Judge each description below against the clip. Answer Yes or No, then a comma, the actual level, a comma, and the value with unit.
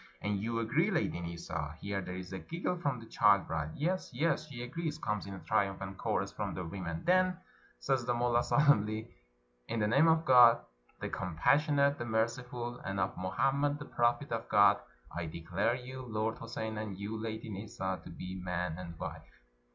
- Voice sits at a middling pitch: No, low, 110 Hz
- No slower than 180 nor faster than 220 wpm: Yes, average, 190 wpm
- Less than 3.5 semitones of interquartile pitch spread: No, wide, 5.5 semitones